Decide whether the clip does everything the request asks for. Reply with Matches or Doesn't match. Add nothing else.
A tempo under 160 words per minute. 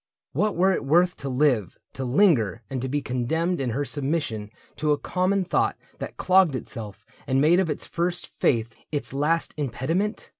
Doesn't match